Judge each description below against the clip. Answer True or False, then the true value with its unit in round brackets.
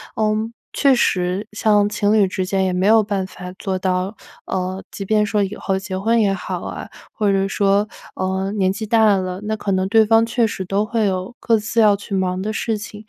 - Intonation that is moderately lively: False (2.2 semitones)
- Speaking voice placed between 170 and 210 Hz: True (200 Hz)